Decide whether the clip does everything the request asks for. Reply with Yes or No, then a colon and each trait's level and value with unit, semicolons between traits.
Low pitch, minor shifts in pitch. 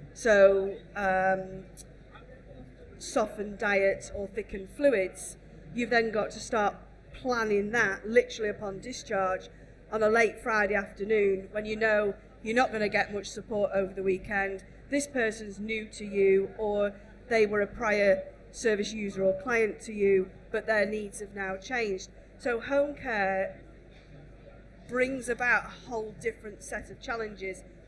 No: high, 210 Hz; narrow, 2.2 semitones